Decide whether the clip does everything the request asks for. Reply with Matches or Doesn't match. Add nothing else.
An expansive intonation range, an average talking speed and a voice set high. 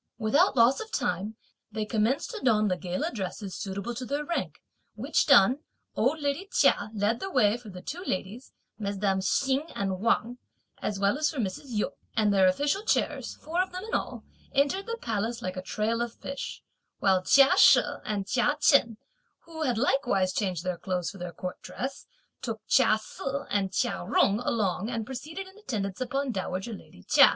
Matches